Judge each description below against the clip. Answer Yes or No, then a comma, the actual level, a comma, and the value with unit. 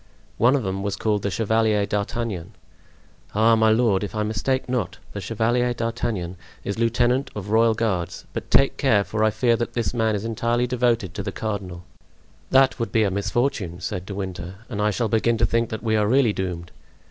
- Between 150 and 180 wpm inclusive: No, average, 200 wpm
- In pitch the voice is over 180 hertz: No, low, 110 Hz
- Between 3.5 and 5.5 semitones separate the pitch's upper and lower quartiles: No, average, 2.7 semitones